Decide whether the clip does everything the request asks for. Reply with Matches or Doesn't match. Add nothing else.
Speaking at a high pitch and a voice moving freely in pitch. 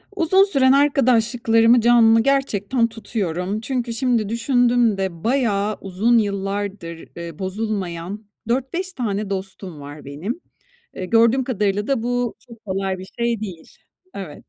Doesn't match